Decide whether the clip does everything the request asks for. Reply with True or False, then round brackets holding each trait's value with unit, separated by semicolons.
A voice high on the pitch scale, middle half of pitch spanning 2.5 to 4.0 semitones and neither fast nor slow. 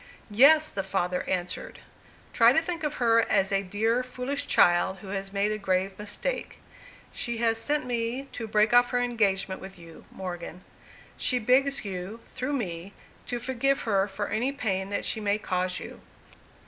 False (215 Hz; 4.5 semitones; 175 wpm)